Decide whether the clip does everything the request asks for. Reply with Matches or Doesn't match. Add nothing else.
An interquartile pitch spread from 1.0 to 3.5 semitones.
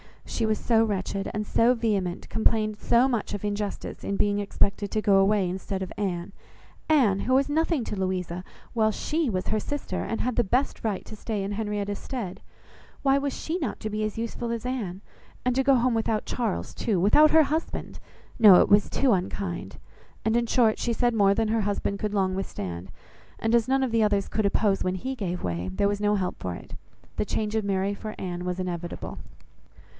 Matches